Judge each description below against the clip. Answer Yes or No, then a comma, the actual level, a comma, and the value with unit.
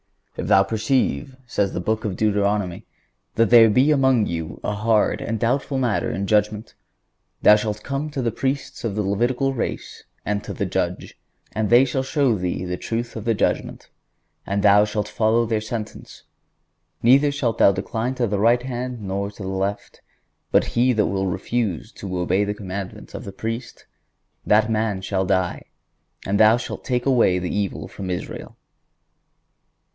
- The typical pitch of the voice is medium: No, low, 110 Hz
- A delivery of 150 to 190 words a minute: Yes, average, 175 wpm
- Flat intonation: No, average, 3.4 semitones